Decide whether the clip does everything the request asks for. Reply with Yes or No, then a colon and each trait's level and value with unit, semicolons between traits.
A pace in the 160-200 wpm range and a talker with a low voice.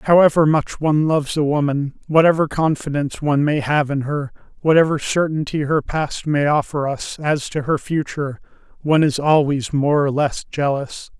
No: average, 165 wpm; medium, 150 Hz